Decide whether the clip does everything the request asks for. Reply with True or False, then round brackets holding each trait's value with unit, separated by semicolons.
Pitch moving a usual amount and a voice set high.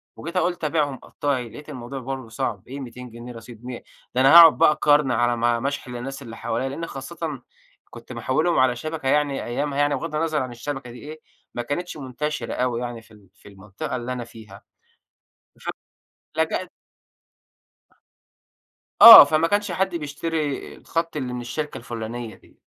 False (4.0 semitones; 135 Hz)